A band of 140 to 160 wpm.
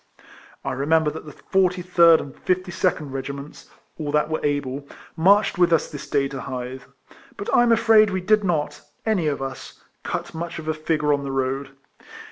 No: average, 180 wpm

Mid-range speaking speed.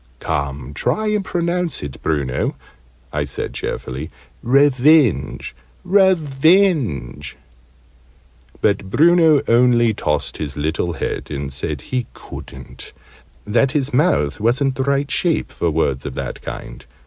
No: slow, 125 wpm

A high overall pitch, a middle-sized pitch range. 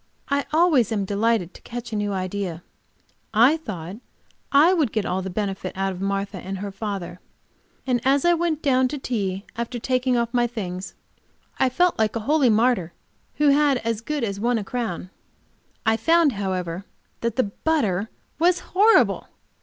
No: high, 225 Hz; wide, 5.8 semitones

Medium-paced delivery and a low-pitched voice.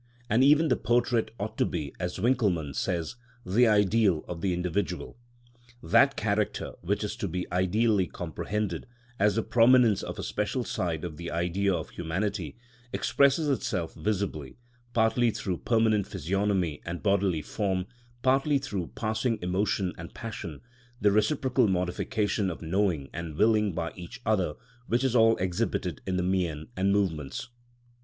Yes: average, 150 wpm; low, 100 Hz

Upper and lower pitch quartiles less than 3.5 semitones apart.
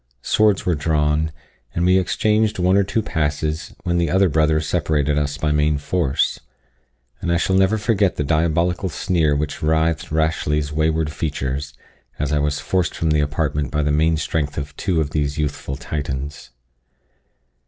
Yes: average, 2.8 semitones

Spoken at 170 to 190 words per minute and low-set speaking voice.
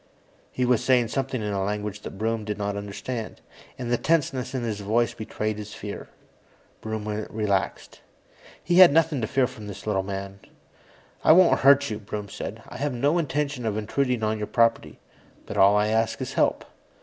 Yes: average, 185 wpm; low, 110 Hz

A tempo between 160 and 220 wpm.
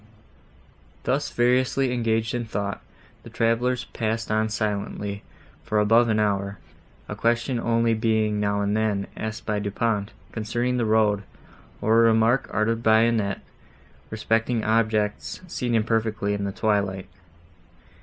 No: slow, 135 wpm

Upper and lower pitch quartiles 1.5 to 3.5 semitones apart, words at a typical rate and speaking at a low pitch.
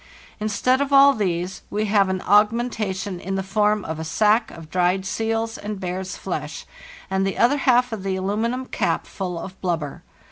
No: average, 3.2 semitones; average, 185 wpm; high, 200 Hz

